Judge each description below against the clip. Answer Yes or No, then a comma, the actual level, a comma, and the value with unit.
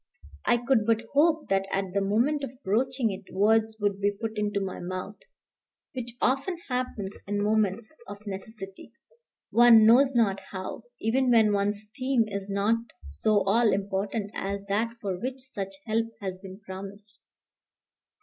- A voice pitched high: Yes, high, 210 Hz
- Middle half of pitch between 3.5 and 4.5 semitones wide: No, average, 3.0 semitones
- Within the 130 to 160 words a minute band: Yes, average, 155 wpm